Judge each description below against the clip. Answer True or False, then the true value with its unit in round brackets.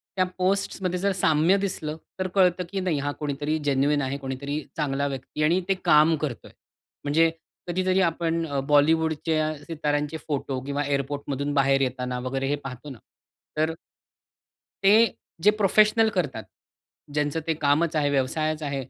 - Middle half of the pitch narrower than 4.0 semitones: True (3.1 semitones)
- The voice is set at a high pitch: False (150 Hz)